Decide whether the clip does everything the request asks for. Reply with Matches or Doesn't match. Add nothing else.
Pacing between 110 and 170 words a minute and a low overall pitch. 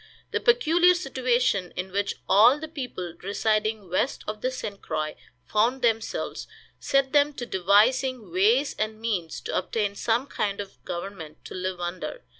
Doesn't match